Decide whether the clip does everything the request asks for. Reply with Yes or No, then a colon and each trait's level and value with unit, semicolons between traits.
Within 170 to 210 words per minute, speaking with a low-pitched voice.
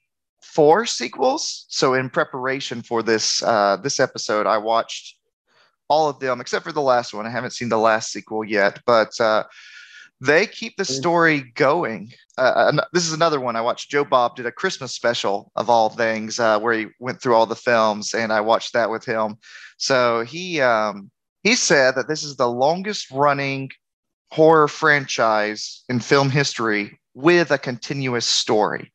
Yes: average, 175 wpm; low, 125 Hz